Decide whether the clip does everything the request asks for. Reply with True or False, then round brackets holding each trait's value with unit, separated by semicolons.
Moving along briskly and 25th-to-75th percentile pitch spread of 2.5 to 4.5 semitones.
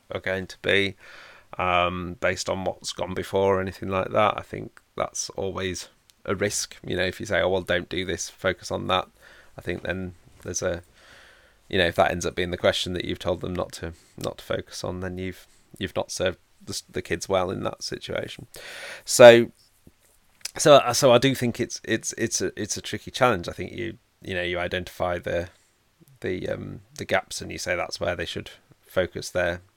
True (210 wpm; 4.1 semitones)